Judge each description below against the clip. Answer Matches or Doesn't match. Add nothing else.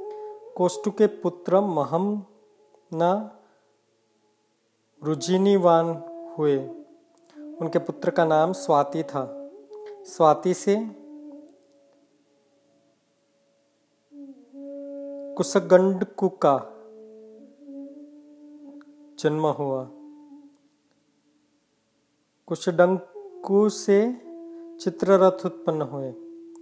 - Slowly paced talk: Matches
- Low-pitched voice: Doesn't match